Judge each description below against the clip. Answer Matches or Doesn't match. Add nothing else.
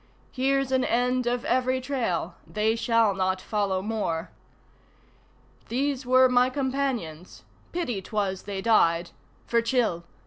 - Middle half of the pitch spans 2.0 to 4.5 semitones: Doesn't match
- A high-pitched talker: Matches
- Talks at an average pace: Doesn't match